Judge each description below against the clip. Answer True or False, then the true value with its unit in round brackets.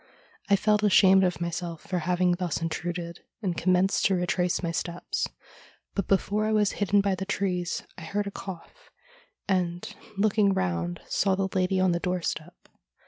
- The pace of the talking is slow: False (165 wpm)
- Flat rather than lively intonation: True (2.2 semitones)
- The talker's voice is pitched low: False (185 Hz)